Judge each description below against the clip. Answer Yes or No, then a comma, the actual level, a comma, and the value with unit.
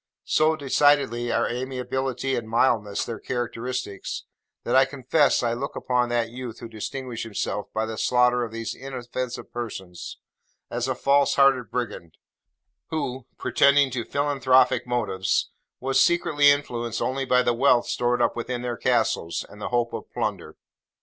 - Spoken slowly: No, average, 150 wpm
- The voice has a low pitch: Yes, low, 125 Hz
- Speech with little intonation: Yes, narrow, 2.2 semitones